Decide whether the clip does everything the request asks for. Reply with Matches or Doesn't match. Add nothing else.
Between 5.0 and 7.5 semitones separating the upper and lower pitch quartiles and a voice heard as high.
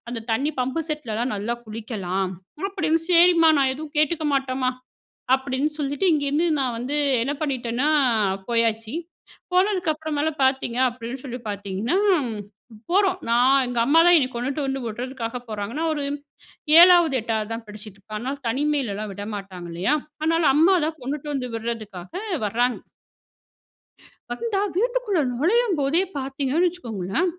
Matches